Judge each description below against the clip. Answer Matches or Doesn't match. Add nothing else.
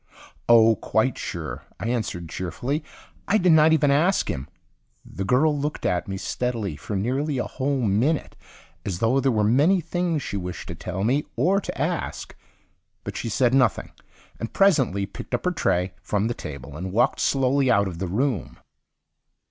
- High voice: Doesn't match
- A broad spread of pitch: Matches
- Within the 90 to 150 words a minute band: Doesn't match